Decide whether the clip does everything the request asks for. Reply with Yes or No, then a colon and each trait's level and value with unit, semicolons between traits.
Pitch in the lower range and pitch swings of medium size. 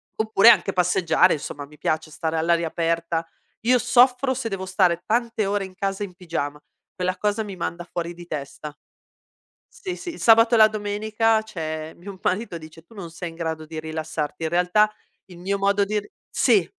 No: medium, 185 Hz; average, 4.5 semitones